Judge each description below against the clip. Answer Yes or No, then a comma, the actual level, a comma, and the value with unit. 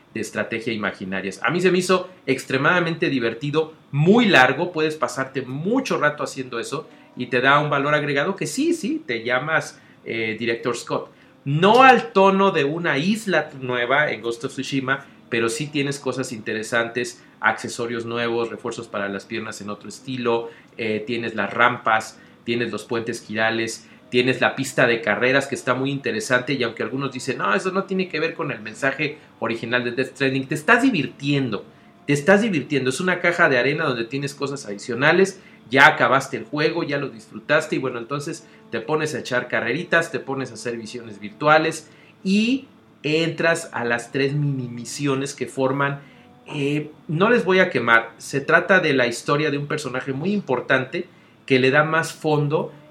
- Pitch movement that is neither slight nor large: Yes, average, 4.9 semitones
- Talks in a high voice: No, low, 135 Hz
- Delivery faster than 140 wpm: Yes, average, 180 wpm